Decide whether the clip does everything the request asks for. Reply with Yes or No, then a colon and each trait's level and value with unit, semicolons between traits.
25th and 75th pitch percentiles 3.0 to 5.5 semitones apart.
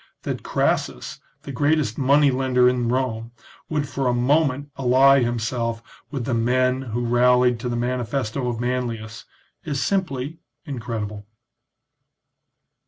No: narrow, 2.5 semitones